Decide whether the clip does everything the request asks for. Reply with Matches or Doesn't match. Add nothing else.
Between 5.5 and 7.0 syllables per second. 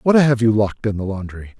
Matches